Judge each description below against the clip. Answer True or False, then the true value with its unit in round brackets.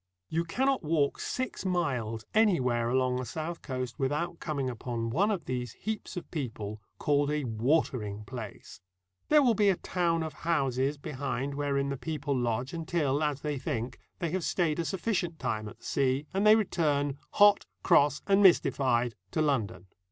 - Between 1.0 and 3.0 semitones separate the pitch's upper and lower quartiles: False (5.1 semitones)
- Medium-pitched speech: True (145 Hz)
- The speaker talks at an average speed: True (170 wpm)